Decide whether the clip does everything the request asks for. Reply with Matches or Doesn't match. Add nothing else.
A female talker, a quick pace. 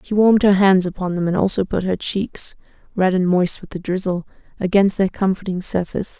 Doesn't match